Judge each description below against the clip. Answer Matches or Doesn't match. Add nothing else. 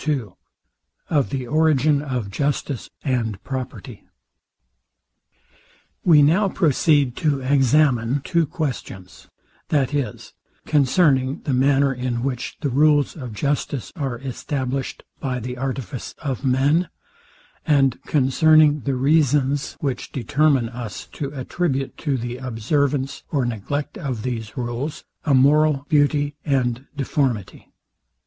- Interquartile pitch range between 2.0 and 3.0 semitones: Matches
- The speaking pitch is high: Doesn't match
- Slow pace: Matches